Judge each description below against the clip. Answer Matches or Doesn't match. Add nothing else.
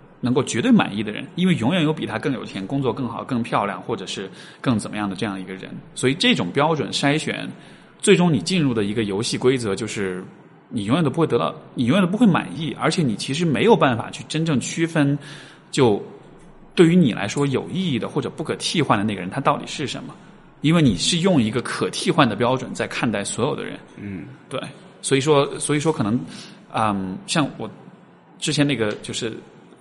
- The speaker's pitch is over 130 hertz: Matches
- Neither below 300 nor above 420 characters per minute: Matches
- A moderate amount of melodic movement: Doesn't match